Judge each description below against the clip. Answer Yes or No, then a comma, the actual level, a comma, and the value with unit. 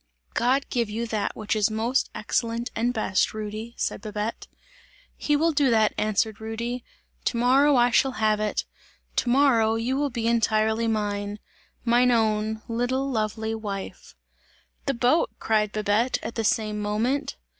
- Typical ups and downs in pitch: No, narrow, 2.3 semitones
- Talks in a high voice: Yes, high, 225 Hz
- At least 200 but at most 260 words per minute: No, average, 155 wpm